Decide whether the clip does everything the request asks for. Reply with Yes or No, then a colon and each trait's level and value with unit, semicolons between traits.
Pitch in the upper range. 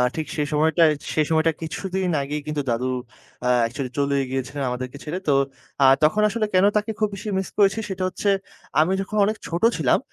No: medium, 160 Hz